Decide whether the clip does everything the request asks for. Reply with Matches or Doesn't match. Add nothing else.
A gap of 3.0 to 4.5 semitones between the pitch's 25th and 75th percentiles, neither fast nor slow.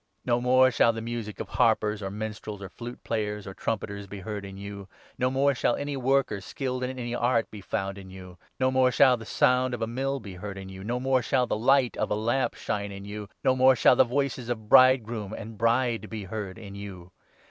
Doesn't match